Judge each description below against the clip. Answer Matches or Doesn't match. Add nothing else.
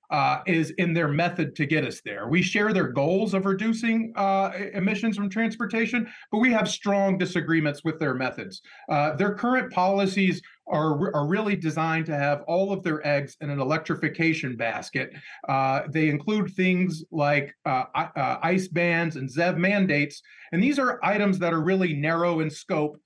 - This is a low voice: Doesn't match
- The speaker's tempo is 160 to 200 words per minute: Matches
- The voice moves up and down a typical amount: Matches